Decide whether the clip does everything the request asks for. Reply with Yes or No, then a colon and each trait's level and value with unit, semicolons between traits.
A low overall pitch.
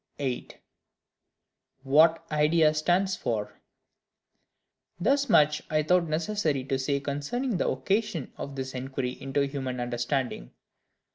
No: medium, 145 Hz